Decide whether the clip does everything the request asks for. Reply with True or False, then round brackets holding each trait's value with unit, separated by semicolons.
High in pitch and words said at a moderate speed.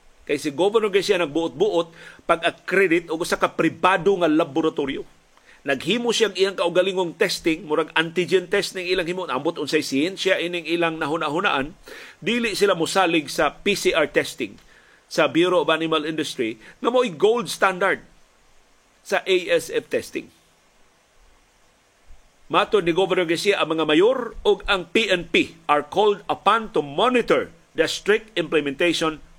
False (180 Hz; 135 wpm)